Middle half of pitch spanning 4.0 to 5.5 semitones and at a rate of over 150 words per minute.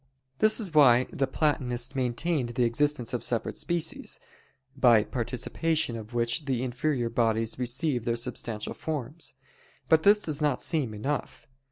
No: average, 4.4 semitones; average, 145 wpm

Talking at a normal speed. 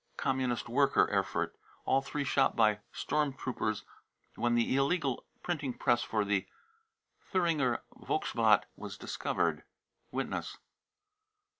No: slow, 115 wpm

